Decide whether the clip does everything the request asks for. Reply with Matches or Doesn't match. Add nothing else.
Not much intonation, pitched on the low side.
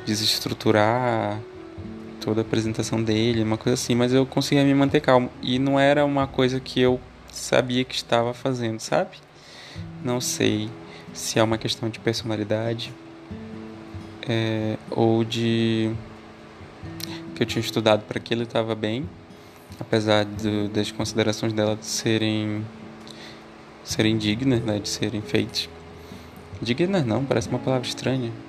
Matches